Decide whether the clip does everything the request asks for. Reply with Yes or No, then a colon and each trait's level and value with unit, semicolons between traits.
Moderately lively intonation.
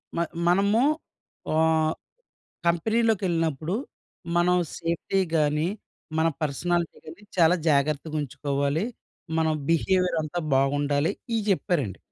Yes: average, 3.2 semitones